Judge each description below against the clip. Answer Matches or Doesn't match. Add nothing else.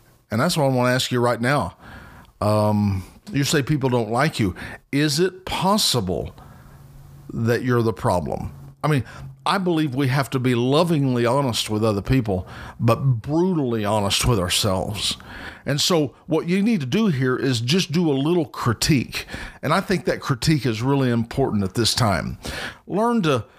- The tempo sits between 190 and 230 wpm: Doesn't match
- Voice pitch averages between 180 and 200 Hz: Doesn't match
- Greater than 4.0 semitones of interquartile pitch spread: Matches